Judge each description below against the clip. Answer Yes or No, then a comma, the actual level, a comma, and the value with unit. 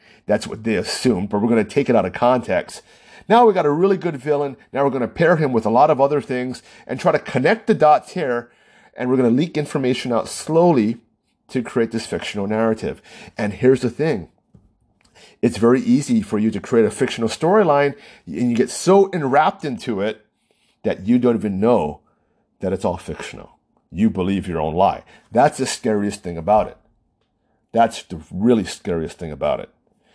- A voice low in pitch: Yes, low, 125 Hz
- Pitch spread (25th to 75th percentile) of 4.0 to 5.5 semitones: Yes, average, 4.7 semitones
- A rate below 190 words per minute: No, average, 200 wpm